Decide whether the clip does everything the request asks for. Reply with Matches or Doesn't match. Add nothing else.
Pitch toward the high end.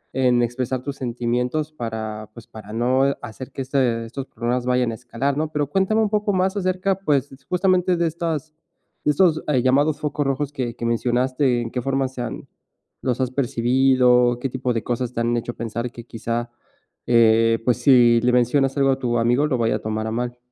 Doesn't match